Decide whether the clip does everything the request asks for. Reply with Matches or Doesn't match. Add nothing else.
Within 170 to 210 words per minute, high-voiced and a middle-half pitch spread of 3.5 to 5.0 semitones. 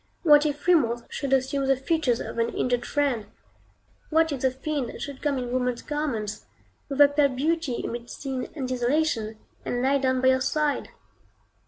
Doesn't match